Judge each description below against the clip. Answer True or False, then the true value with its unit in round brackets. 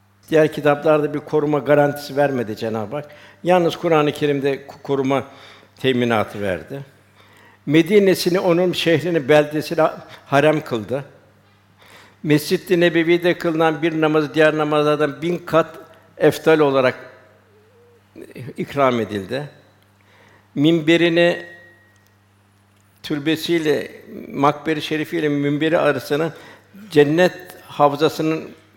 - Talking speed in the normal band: False (90 wpm)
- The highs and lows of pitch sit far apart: True (6.1 semitones)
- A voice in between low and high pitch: True (145 Hz)